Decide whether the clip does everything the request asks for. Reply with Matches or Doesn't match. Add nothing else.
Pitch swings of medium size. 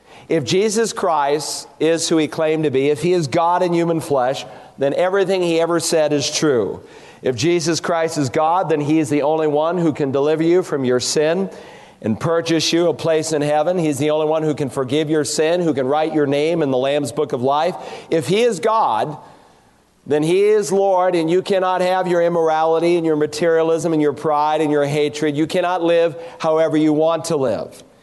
Doesn't match